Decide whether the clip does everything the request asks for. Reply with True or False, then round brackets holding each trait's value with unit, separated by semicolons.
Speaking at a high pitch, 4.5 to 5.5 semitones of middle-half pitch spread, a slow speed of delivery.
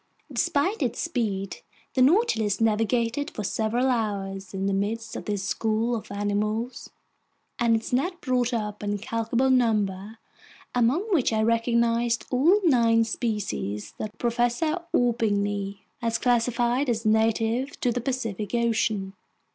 False (230 Hz; 2.8 semitones; 130 wpm)